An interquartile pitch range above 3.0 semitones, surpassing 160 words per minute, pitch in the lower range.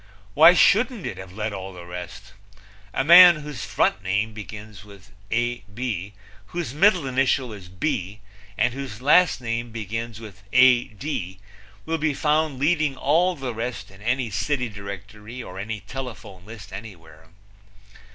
No: wide, 5.5 semitones; average, 145 wpm; low, 115 Hz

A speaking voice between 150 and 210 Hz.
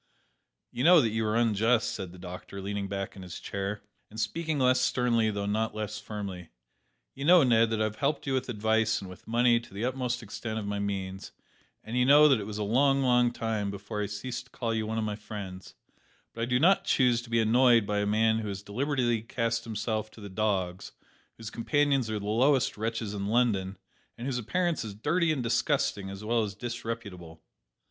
No: low, 110 Hz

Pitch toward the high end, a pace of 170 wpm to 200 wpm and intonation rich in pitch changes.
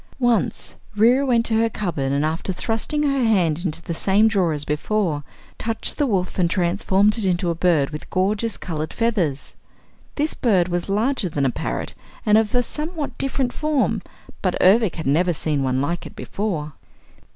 Yes: high, 195 Hz; average, 180 wpm; wide, 5.7 semitones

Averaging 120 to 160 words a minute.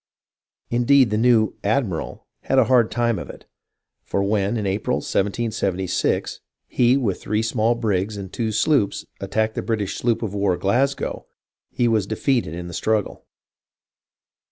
Yes: average, 155 wpm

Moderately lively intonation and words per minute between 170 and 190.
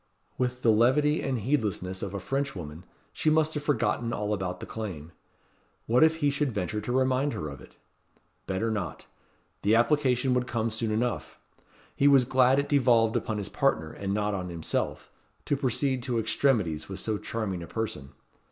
Yes: average, 4.9 semitones; average, 180 wpm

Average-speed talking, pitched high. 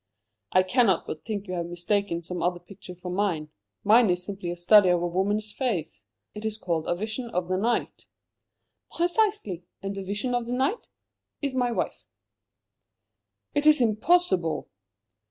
Yes: average, 165 wpm; high, 200 Hz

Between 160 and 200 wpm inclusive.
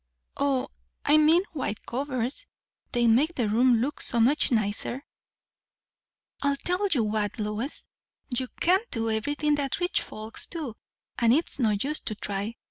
No: average, 150 wpm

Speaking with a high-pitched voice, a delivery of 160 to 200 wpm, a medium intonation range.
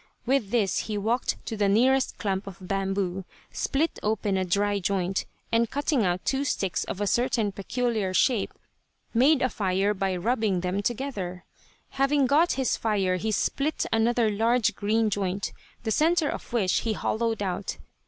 Yes: high, 215 Hz; average, 165 wpm; average, 4.0 semitones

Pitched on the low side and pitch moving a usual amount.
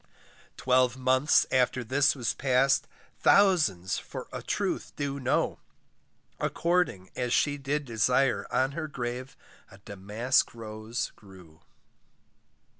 Yes: low, 130 Hz; average, 3.9 semitones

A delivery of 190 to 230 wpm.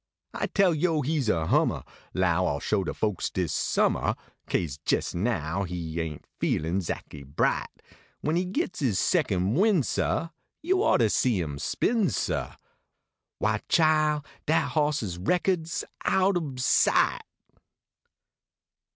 No: average, 150 wpm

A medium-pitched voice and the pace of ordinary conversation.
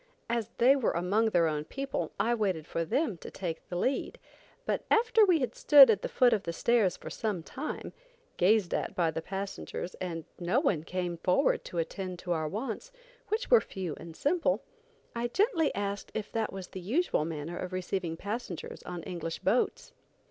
No: high, 195 Hz; average, 190 wpm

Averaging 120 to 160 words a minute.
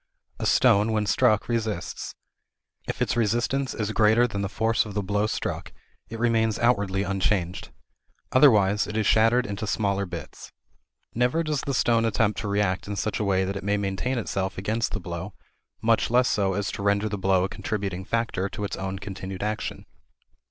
No: average, 185 wpm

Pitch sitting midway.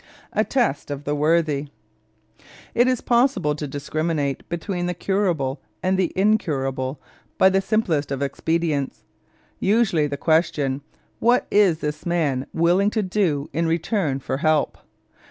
Yes: medium, 160 Hz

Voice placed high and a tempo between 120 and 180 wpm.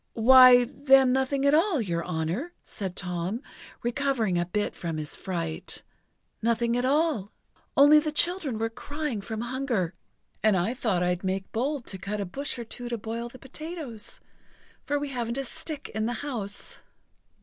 Yes: high, 235 Hz; average, 170 wpm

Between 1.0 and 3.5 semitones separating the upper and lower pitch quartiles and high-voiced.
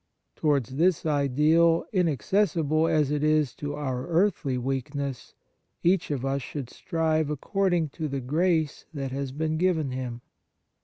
No: average, 3.2 semitones; medium, 150 Hz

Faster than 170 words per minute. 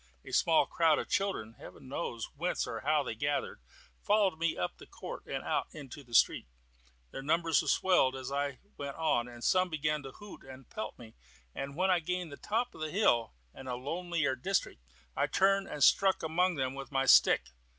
Yes: average, 200 wpm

